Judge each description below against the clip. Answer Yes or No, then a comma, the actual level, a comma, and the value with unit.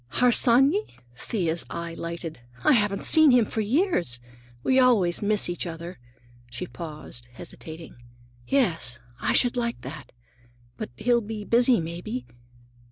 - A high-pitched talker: Yes, high, 205 Hz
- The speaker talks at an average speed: No, slow, 130 wpm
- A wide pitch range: Yes, wide, 6.7 semitones